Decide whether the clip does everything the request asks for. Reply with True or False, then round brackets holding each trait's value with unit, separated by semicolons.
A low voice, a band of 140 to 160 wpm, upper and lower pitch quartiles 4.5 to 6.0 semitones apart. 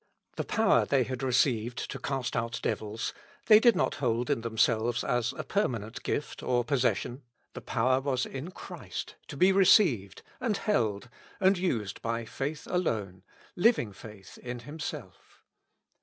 True (125 Hz; 150 wpm; 5.6 semitones)